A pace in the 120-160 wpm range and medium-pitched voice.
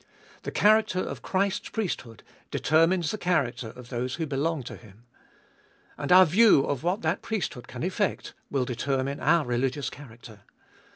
Yes: average, 155 wpm; medium, 145 Hz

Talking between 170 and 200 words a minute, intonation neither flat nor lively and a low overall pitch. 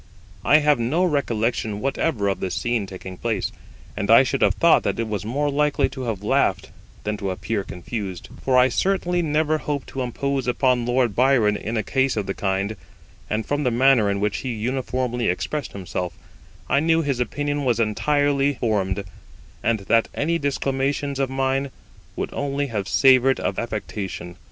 Yes: average, 175 wpm; average, 4.9 semitones; low, 125 Hz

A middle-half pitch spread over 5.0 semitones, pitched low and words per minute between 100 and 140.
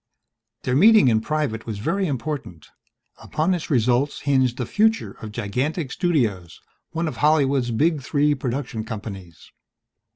Yes: wide, 5.5 semitones; low, 130 Hz; slow, 135 wpm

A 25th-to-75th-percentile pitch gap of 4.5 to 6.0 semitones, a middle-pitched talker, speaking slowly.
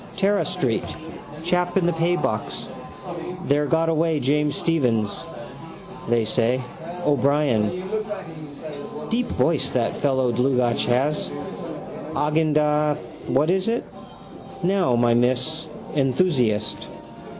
Yes: average, 5.0 semitones; medium, 150 Hz; slow, 95 wpm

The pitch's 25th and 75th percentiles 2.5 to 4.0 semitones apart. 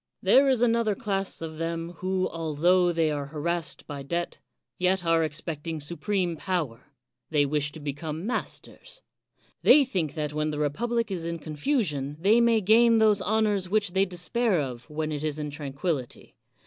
No: average, 5.1 semitones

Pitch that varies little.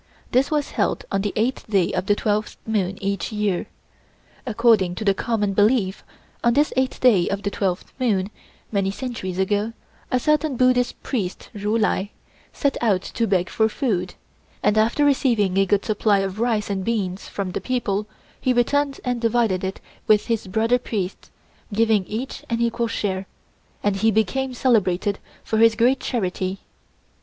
No: average, 3.5 semitones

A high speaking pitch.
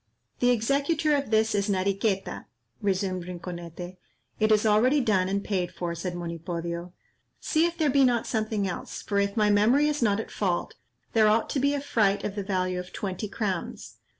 Yes: high, 205 Hz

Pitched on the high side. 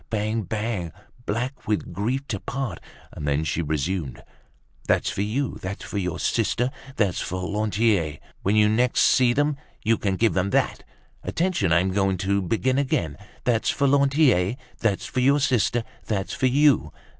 No: low, 105 Hz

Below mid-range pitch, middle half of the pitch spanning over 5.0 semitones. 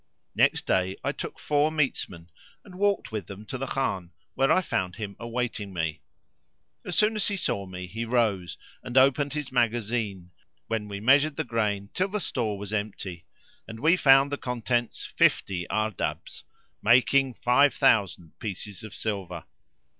Yes: low, 115 Hz; wide, 5.4 semitones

